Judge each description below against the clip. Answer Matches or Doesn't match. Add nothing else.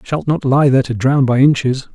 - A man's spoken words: Matches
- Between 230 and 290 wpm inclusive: Matches